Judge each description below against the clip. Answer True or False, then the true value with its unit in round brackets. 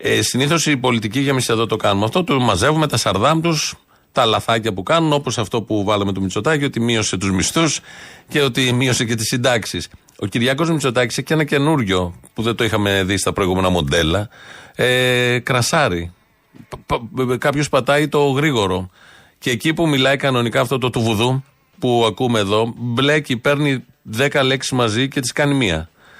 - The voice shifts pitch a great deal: False (4.5 semitones)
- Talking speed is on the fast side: True (175 wpm)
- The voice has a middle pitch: False (125 Hz)